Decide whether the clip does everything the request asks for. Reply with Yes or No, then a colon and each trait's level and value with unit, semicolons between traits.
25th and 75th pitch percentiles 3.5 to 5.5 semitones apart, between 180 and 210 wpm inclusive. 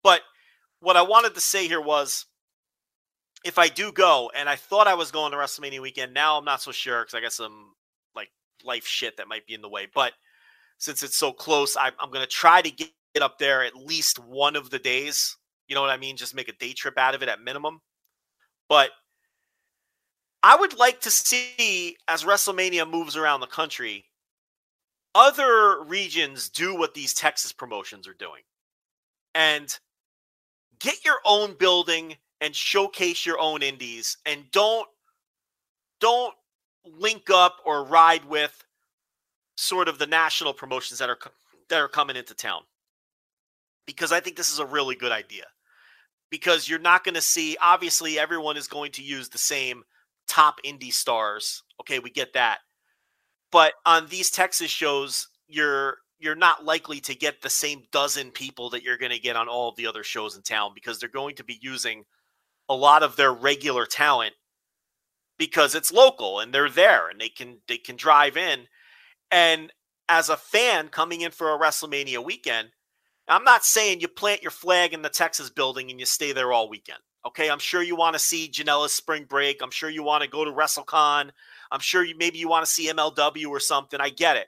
Yes: average, 4.1 semitones; average, 190 wpm